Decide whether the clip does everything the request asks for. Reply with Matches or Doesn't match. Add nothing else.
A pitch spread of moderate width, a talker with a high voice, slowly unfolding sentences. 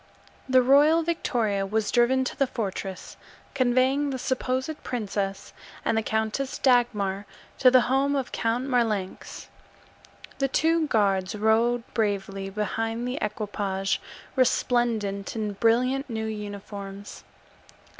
Matches